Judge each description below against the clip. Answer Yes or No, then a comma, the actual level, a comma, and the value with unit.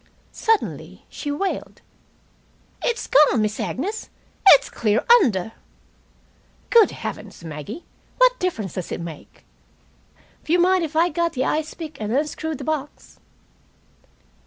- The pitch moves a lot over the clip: Yes, wide, 8.1 semitones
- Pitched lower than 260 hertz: No, very high, 305 Hz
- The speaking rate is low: Yes, slow, 125 wpm